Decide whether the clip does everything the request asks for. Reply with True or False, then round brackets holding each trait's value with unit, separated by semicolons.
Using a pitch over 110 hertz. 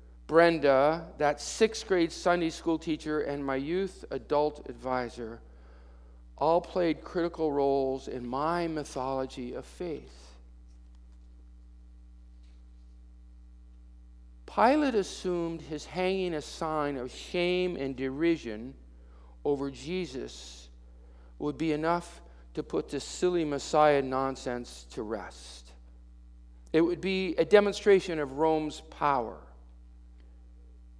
True (135 Hz)